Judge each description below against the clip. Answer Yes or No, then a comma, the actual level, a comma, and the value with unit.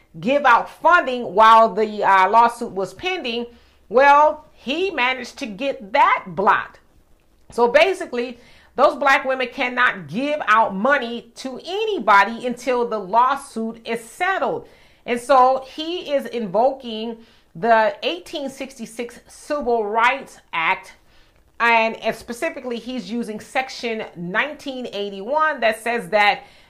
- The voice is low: No, high, 240 Hz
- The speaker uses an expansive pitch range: No, average, 3.7 semitones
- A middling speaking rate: No, slow, 115 wpm